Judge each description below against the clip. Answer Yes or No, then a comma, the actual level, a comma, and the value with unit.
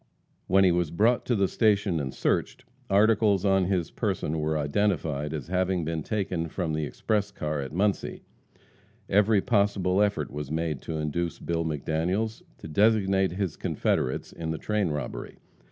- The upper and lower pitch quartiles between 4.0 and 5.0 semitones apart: Yes, average, 4.5 semitones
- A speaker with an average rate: Yes, average, 160 wpm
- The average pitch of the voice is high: No, very low, 90 Hz